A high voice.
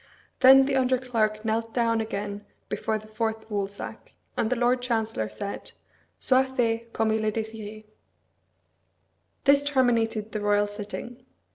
Yes: high, 225 Hz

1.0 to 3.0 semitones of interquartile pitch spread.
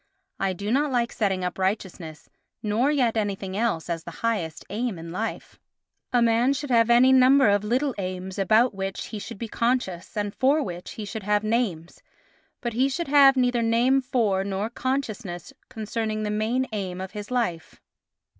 No: average, 4.3 semitones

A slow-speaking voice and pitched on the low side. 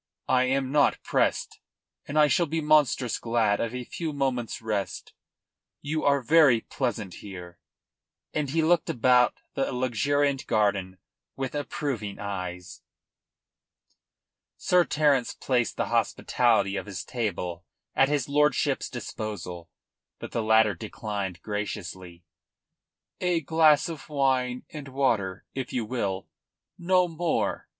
Yes: slow, 125 wpm; low, 125 Hz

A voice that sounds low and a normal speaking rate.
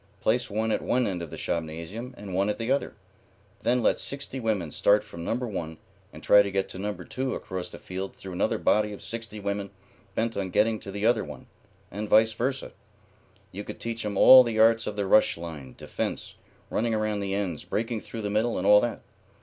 No: low, 105 Hz; fast, 215 wpm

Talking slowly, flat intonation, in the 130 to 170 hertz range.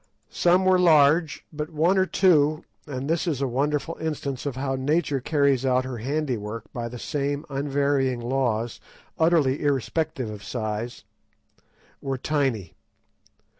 No: slow, 130 wpm; average, 3.4 semitones; medium, 140 Hz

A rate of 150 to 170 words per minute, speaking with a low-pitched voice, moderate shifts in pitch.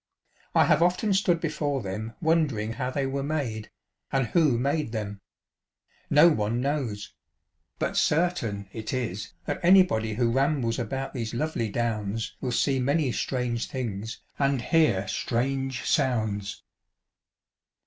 No: slow, 135 wpm; low, 125 Hz; average, 4.9 semitones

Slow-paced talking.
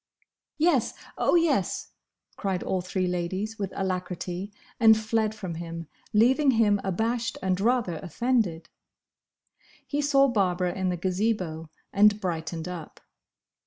Yes: slow, 125 wpm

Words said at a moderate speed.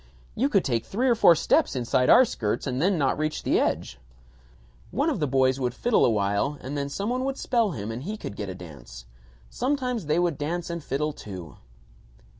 No: fast, 215 wpm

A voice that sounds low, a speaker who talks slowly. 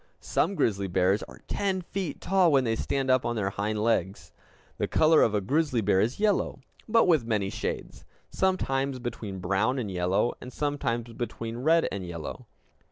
No: low, 120 Hz; average, 175 wpm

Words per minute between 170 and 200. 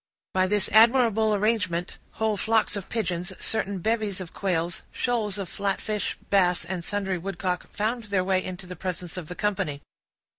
No: average, 160 wpm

